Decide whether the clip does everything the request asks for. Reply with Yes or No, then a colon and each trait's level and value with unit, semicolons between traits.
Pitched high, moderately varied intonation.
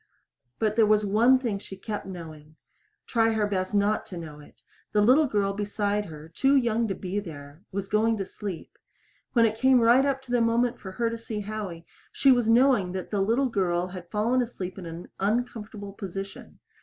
Yes: high, 210 Hz; average, 3.5 semitones